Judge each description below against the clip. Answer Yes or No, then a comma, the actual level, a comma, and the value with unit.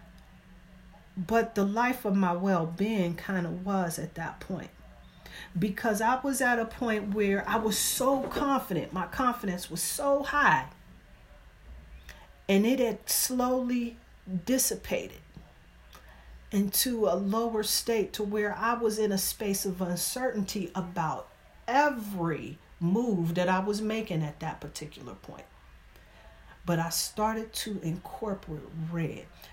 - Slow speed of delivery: Yes, slow, 130 wpm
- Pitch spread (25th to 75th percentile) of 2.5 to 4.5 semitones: No, average, 5.3 semitones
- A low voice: No, high, 195 Hz